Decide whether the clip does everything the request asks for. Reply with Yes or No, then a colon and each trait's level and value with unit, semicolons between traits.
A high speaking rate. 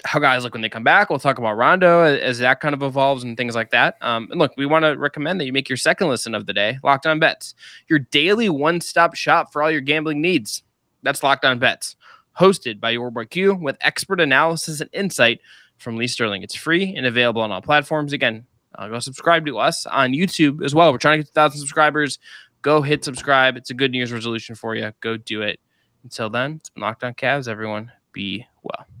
Yes: fast, 230 wpm